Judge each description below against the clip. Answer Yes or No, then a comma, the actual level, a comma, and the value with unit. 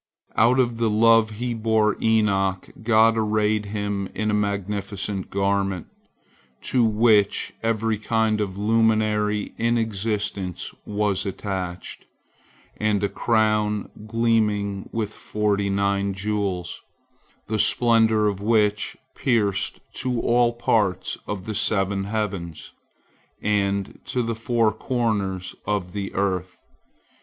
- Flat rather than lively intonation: Yes, narrow, 2.1 semitones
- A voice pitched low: Yes, low, 105 Hz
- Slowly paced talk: Yes, slow, 115 wpm